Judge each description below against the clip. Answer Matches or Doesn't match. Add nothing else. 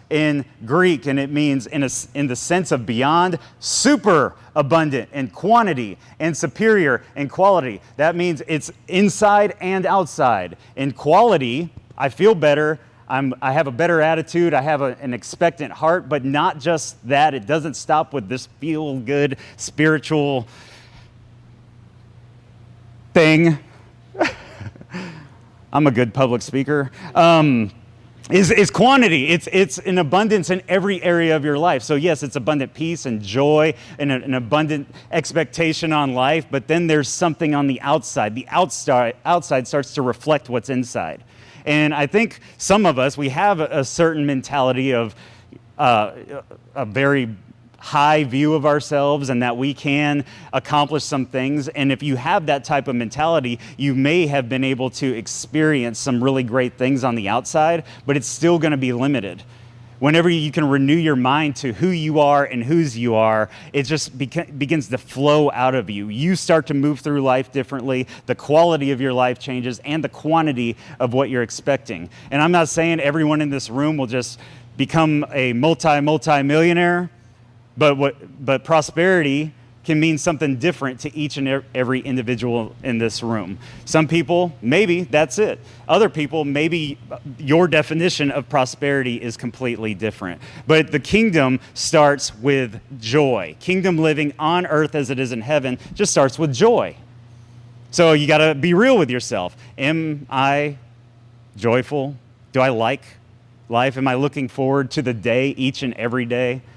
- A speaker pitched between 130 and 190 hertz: Matches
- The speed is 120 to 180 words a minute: Matches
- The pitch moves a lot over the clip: Doesn't match